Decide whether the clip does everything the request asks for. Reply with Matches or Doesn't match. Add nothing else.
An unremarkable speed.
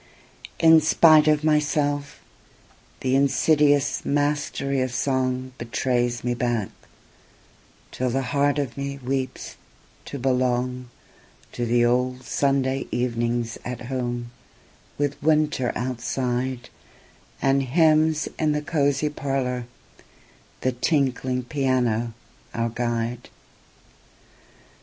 Doesn't match